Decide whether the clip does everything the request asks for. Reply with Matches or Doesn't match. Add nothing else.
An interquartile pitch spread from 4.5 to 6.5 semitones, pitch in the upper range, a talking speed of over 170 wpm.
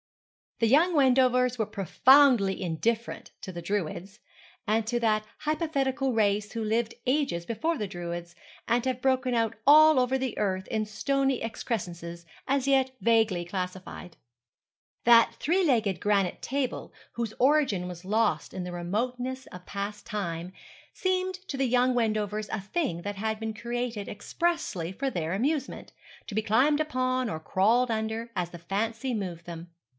Doesn't match